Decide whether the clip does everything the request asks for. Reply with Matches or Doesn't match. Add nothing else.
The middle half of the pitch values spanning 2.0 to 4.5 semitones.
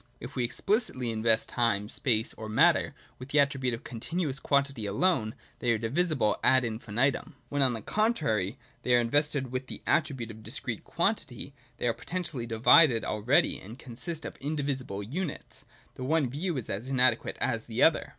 Matches